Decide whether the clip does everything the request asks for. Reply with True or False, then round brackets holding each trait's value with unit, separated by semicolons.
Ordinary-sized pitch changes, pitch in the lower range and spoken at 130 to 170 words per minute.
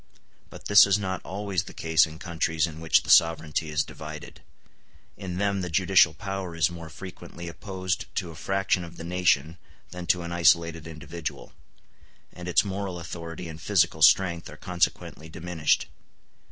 False (2.3 semitones; 85 Hz; 165 wpm)